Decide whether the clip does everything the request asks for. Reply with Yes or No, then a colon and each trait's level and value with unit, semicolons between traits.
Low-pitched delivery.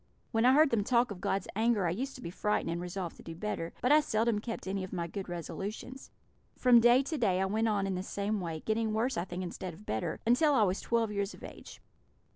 No: high, 210 Hz